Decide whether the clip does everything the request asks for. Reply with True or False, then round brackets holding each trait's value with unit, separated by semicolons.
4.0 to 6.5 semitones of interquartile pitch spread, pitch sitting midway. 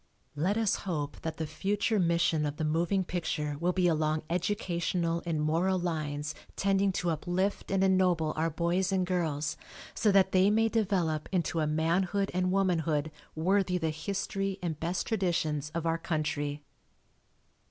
False (3.3 semitones; 170 Hz)